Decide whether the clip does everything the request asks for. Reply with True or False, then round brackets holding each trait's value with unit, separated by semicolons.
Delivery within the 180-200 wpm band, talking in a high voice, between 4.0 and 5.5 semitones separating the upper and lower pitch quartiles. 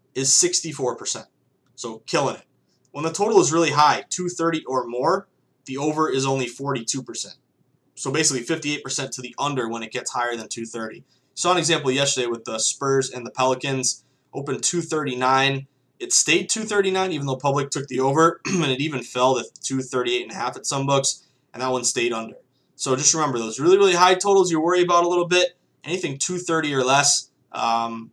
False (190 wpm; 135 Hz; 4.3 semitones)